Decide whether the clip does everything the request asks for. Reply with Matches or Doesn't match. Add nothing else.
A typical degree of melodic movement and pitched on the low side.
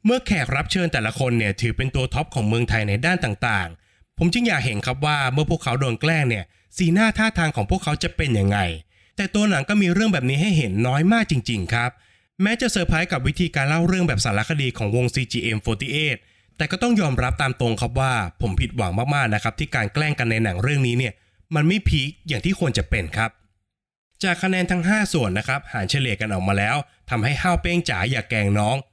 Doesn't match